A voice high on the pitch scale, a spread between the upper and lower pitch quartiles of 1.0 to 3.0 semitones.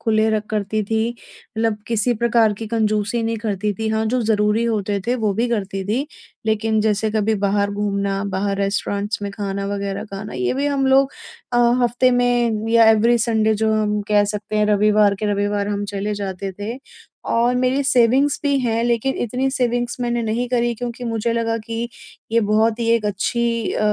Yes: high, 220 Hz; narrow, 2.4 semitones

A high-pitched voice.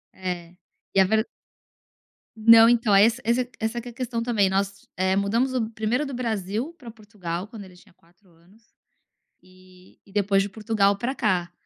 Yes: high, 210 Hz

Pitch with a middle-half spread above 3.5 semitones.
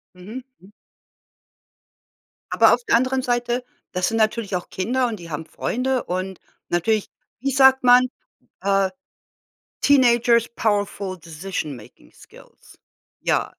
Yes: average, 5.1 semitones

